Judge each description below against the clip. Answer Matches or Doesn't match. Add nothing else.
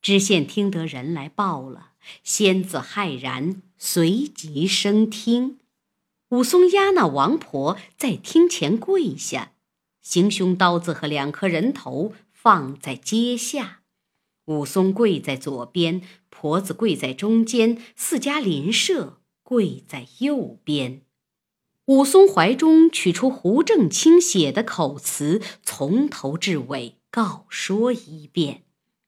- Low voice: Doesn't match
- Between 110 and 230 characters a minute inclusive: Matches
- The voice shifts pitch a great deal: Matches